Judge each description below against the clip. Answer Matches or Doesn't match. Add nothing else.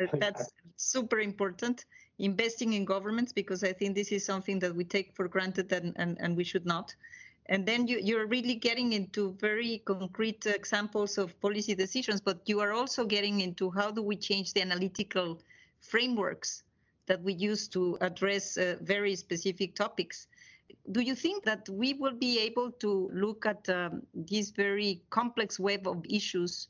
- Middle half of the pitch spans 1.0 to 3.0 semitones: Matches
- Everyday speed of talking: Matches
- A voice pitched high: Matches